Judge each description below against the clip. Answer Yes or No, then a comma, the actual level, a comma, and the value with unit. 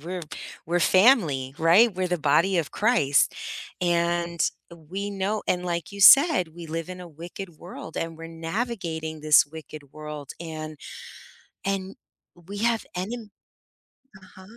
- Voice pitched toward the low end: No, medium, 175 Hz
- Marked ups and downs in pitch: No, average, 3.4 semitones